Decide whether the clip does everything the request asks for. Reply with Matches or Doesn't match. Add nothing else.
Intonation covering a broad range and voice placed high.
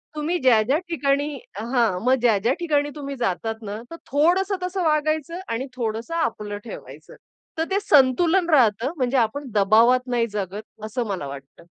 Matches